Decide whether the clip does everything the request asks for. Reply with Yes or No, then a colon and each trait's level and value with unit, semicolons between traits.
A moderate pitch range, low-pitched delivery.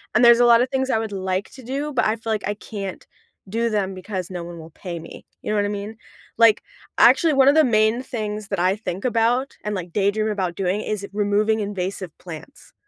No: average, 3.4 semitones; high, 210 Hz